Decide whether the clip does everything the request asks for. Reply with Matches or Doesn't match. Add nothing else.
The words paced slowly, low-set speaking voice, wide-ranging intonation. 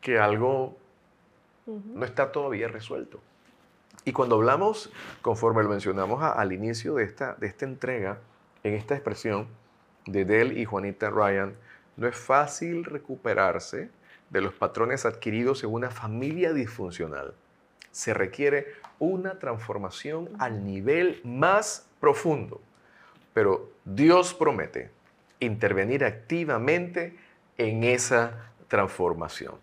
Matches